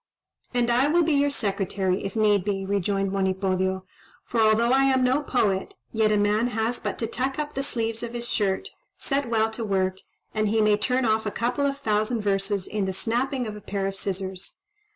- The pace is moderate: No, fast, 210 wpm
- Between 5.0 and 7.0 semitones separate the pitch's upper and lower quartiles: No, average, 3.9 semitones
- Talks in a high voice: Yes, high, 215 Hz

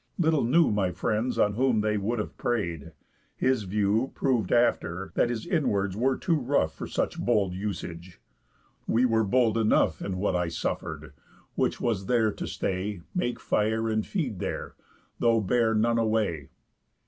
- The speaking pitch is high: No, low, 110 Hz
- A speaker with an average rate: Yes, average, 160 wpm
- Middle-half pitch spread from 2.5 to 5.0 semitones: Yes, average, 3.8 semitones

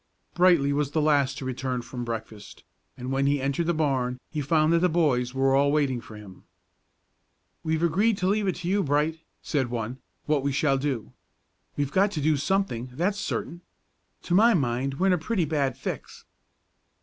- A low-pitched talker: No, medium, 145 Hz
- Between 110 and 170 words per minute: No, average, 190 wpm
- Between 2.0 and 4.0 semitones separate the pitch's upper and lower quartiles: No, average, 4.6 semitones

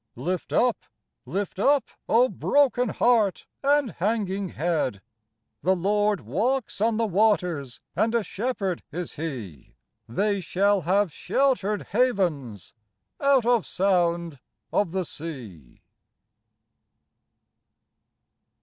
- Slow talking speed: Yes, slow, 105 wpm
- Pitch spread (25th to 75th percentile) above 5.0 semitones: Yes, wide, 5.4 semitones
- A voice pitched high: Yes, high, 195 Hz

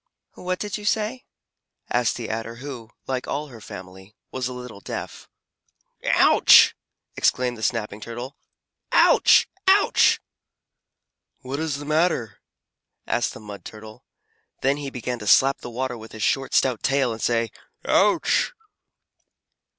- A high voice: No, low, 125 Hz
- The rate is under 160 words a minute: Yes, average, 140 wpm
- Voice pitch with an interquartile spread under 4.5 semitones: Yes, average, 4.0 semitones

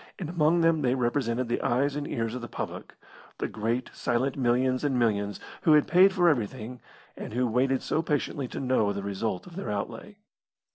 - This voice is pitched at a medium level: No, low, 125 Hz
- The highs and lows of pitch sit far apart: No, average, 4.3 semitones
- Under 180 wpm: No, average, 195 wpm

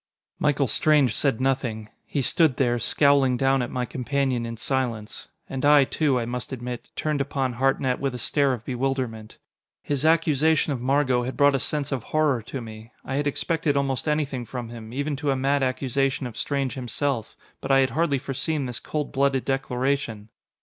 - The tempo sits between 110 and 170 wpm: No, average, 185 wpm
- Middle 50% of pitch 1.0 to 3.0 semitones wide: Yes, narrow, 2.4 semitones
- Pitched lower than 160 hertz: Yes, low, 135 Hz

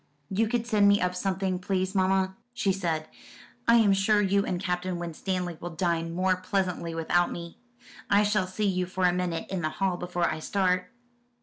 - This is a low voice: No, medium, 185 Hz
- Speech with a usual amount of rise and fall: No, narrow, 1.8 semitones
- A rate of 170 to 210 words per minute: Yes, average, 190 wpm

